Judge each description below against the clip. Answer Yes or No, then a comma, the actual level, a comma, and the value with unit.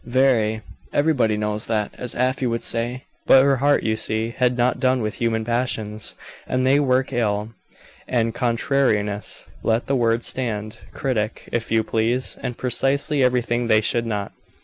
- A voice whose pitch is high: No, low, 120 Hz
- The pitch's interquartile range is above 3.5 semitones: No, average, 2.7 semitones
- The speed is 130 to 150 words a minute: No, average, 160 wpm